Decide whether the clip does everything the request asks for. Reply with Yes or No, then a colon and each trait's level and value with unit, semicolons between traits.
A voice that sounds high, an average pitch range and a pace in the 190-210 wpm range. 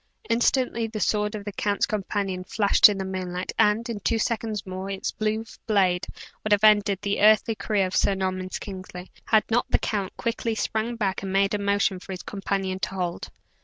No: high, 200 Hz; narrow, 2.3 semitones; average, 200 wpm